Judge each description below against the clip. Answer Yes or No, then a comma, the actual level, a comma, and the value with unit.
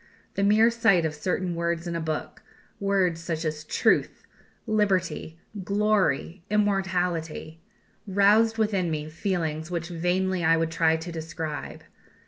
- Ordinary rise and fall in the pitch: Yes, average, 3.5 semitones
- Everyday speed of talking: No, slow, 130 wpm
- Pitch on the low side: No, medium, 175 Hz